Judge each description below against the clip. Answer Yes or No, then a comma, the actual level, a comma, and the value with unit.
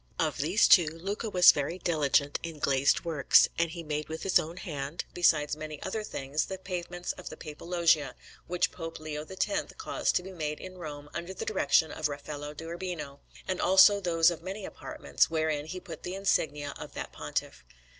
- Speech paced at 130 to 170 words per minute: No, average, 195 wpm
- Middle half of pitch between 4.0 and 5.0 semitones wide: No, average, 3.3 semitones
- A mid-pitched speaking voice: Yes, medium, 165 Hz